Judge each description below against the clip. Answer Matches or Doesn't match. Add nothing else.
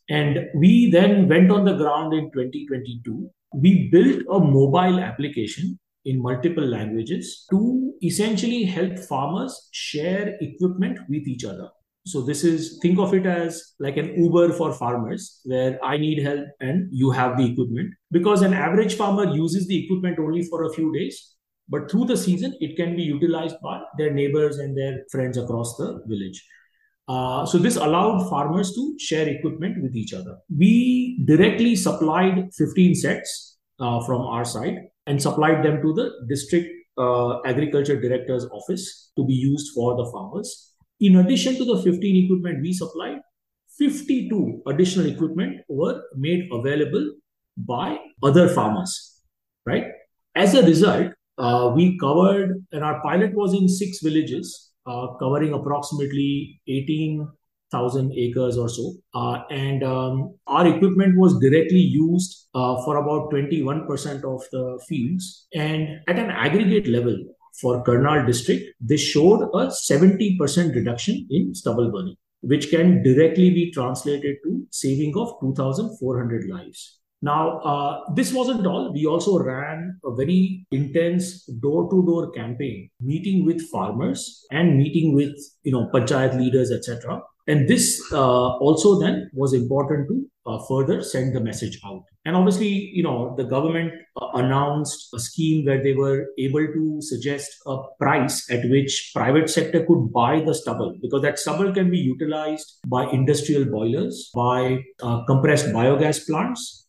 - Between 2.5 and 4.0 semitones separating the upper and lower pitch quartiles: Doesn't match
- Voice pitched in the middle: Matches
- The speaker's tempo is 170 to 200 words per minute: Doesn't match